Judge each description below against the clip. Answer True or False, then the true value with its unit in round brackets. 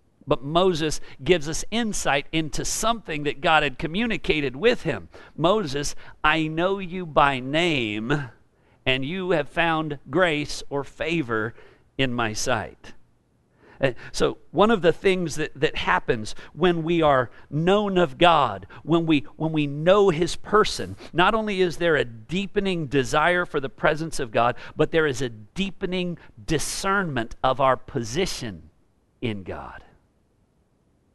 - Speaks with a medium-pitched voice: True (155 Hz)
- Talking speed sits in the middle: True (145 wpm)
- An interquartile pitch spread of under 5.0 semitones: False (5.3 semitones)